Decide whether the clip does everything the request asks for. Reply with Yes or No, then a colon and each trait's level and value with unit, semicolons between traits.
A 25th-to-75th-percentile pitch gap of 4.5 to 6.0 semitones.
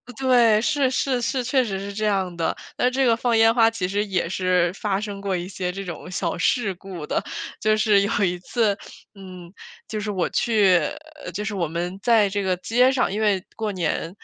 No: average, 3.7 semitones